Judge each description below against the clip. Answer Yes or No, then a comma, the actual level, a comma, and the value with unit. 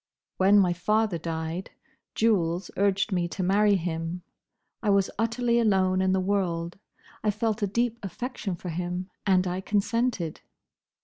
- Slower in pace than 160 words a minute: Yes, average, 145 wpm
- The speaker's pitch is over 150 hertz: Yes, high, 190 Hz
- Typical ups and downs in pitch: Yes, average, 3.1 semitones